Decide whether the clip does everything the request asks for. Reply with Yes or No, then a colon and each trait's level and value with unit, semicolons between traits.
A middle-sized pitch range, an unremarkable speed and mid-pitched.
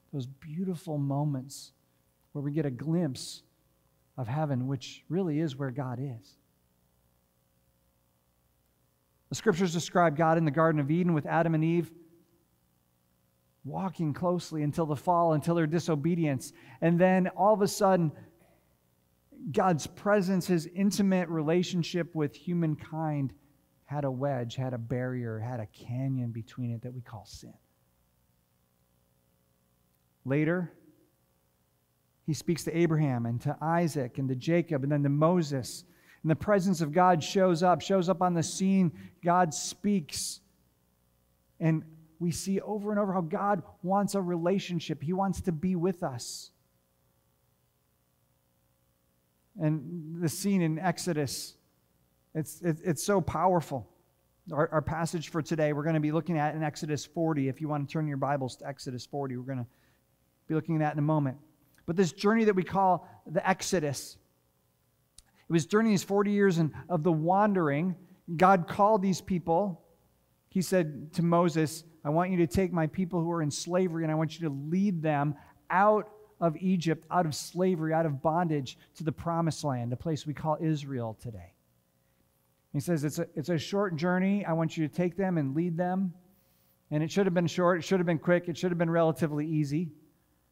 No: wide, 6.3 semitones; average, 165 wpm; medium, 155 Hz